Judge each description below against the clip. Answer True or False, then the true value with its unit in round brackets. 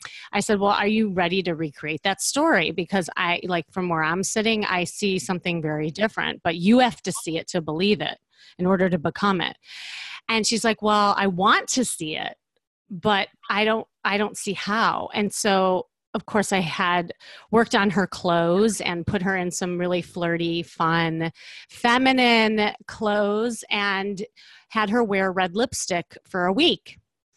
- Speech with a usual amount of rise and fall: True (3.4 semitones)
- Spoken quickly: False (180 wpm)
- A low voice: False (195 Hz)